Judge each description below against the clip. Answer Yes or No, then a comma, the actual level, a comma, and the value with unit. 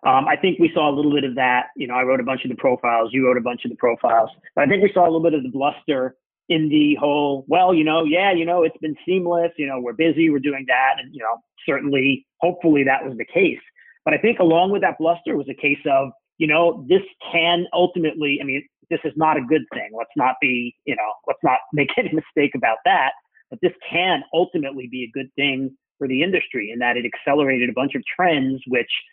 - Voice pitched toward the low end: No, medium, 150 Hz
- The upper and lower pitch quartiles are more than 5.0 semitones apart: No, average, 4.1 semitones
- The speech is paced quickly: Yes, fast, 250 wpm